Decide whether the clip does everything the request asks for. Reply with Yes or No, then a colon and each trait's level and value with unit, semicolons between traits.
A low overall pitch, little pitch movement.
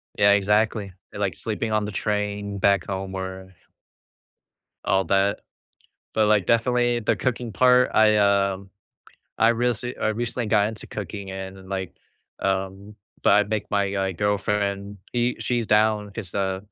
Yes: low, 105 Hz; narrow, 2.0 semitones